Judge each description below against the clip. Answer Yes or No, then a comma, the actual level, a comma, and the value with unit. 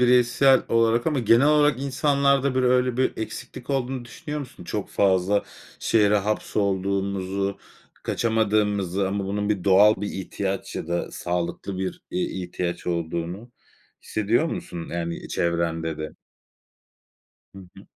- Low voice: Yes, low, 105 Hz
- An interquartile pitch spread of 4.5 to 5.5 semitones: Yes, average, 4.9 semitones